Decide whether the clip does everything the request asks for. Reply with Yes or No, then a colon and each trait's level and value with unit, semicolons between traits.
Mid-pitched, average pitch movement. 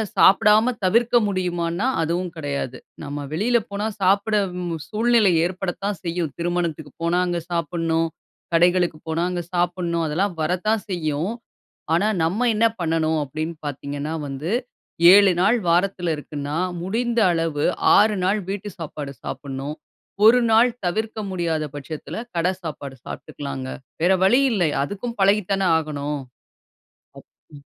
Yes: medium, 175 Hz; average, 4.2 semitones